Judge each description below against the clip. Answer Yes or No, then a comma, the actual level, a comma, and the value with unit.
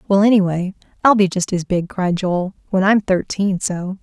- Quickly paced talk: No, average, 195 wpm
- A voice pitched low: No, high, 190 Hz